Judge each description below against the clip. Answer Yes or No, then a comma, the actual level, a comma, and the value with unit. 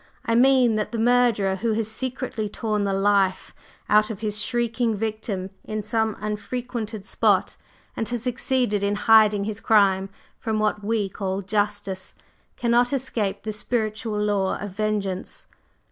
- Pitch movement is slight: Yes, narrow, 2.1 semitones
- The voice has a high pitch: Yes, high, 215 Hz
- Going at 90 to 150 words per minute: Yes, average, 145 wpm